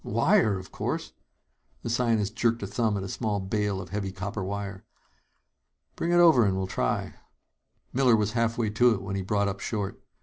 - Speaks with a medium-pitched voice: No, low, 105 Hz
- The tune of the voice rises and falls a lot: No, average, 3.0 semitones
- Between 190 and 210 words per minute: Yes, average, 195 wpm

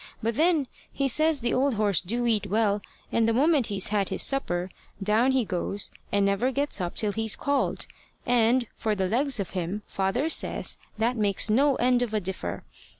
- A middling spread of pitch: Yes, average, 4.4 semitones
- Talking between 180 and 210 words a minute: Yes, average, 195 wpm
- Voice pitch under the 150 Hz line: No, high, 225 Hz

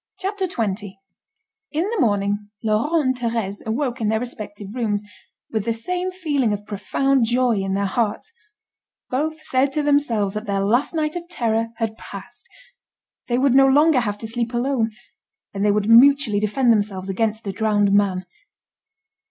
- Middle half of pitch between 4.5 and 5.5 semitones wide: Yes, average, 4.8 semitones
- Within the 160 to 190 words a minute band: Yes, average, 165 wpm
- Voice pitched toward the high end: Yes, high, 230 Hz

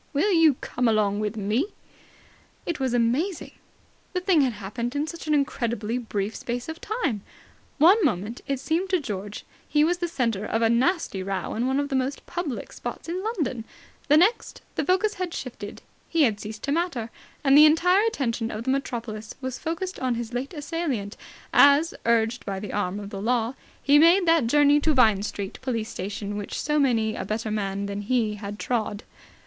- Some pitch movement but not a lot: No, wide, 6.4 semitones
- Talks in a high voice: Yes, very high, 250 Hz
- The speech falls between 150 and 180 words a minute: No, average, 195 wpm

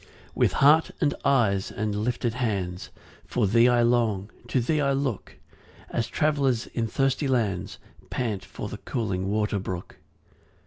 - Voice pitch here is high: No, low, 115 Hz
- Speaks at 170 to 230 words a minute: No, average, 150 wpm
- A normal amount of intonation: Yes, average, 4.6 semitones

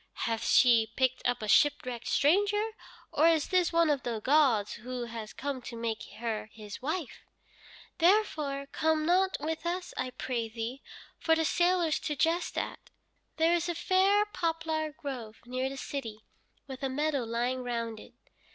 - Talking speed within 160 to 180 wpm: Yes, average, 165 wpm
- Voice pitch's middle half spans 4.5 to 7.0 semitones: Yes, wide, 5.6 semitones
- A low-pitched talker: No, very high, 280 Hz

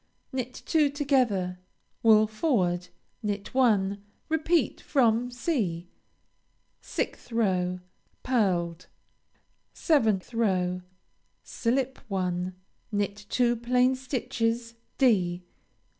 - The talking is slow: Yes, slow, 85 wpm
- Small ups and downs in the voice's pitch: No, average, 5.3 semitones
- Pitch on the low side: No, high, 225 Hz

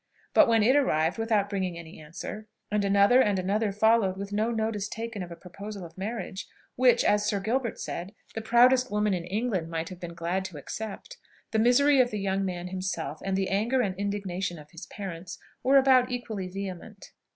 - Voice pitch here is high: Yes, high, 200 Hz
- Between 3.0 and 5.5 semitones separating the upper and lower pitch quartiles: Yes, average, 3.5 semitones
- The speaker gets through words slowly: No, average, 195 wpm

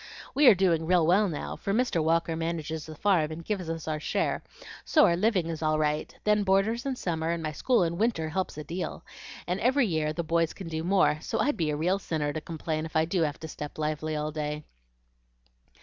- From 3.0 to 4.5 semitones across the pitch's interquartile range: Yes, average, 3.5 semitones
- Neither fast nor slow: No, fast, 225 wpm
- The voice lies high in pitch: No, medium, 165 Hz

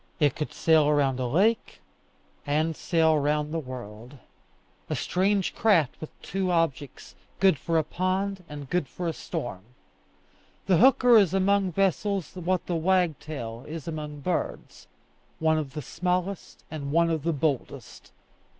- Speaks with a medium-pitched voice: Yes, medium, 160 Hz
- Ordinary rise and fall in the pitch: Yes, average, 4.0 semitones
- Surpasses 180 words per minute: No, average, 150 wpm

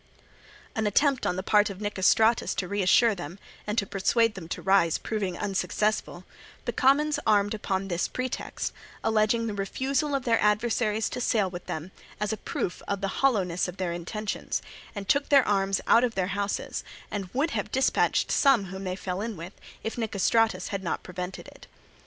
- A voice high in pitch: Yes, high, 205 Hz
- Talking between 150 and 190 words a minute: Yes, average, 180 wpm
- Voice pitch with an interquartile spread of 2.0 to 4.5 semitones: Yes, average, 3.2 semitones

